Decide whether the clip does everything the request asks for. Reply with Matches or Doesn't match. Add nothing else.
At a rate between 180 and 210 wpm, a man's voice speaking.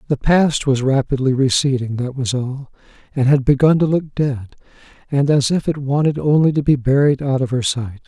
Matches